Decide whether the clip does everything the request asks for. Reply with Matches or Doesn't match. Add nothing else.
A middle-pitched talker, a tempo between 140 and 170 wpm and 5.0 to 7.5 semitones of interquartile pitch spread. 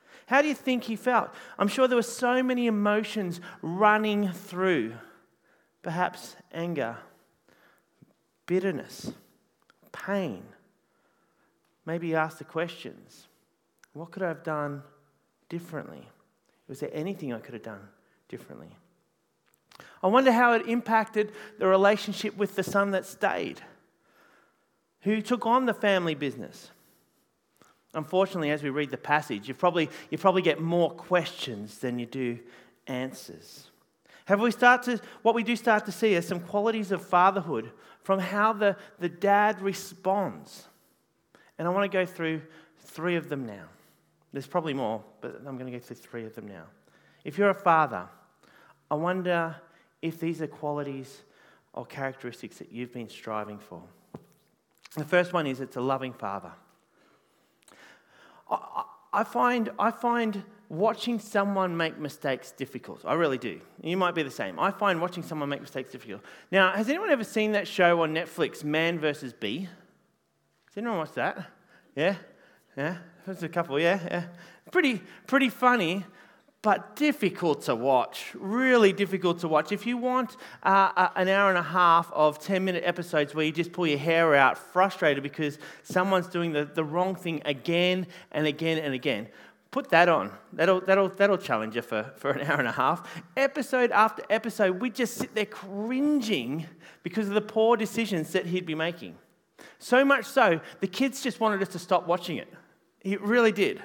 Matches